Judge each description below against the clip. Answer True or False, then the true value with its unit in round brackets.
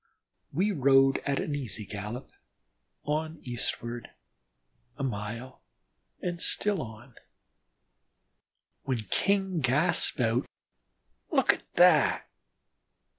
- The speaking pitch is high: False (135 Hz)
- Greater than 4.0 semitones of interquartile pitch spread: True (5.2 semitones)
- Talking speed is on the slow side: True (90 wpm)